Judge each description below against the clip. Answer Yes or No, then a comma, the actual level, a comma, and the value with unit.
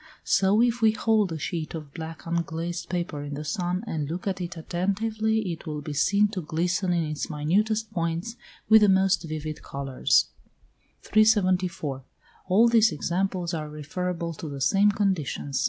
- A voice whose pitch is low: No, medium, 175 Hz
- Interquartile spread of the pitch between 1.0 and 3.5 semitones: No, average, 4.5 semitones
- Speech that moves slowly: No, average, 165 wpm